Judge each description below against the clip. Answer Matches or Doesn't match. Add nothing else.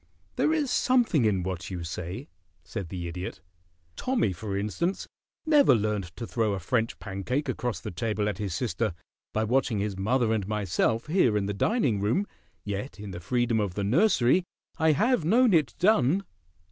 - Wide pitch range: Matches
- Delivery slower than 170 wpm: Doesn't match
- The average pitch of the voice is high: Doesn't match